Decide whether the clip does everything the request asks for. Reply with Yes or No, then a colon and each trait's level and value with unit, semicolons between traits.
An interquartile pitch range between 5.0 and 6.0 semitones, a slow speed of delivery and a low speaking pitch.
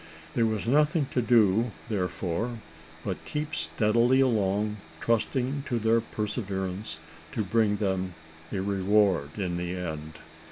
No: average, 3.7 semitones; slow, 125 wpm; low, 105 Hz